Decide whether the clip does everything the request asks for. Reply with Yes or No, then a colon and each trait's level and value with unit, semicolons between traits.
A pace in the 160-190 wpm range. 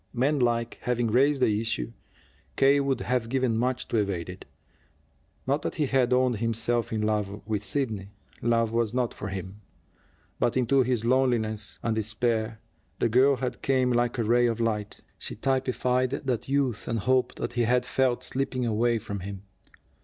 Yes: average, 170 wpm